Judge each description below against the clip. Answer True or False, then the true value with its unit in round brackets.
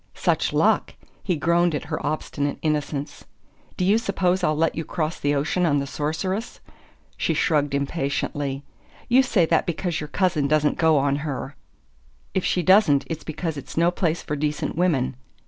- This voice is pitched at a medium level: True (155 Hz)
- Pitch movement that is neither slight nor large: True (3.5 semitones)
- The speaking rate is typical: True (170 wpm)